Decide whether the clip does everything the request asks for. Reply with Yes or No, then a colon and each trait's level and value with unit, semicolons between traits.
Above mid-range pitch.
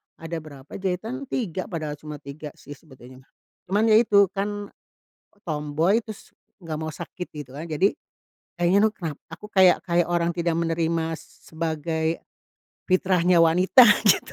No: medium, 170 Hz